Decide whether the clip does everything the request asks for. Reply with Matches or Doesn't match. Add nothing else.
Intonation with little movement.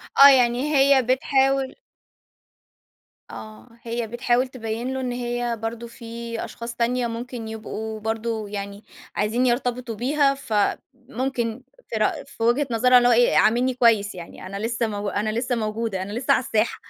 Matches